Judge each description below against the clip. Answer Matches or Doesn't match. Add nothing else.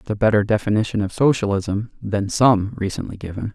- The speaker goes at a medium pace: Matches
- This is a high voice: Doesn't match